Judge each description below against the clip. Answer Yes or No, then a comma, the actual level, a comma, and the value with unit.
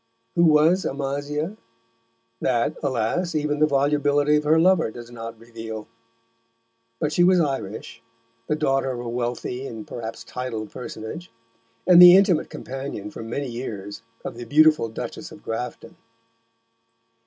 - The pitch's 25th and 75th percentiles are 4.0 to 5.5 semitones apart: Yes, average, 4.8 semitones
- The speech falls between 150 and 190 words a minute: No, average, 140 wpm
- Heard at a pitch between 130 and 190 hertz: Yes, low, 135 Hz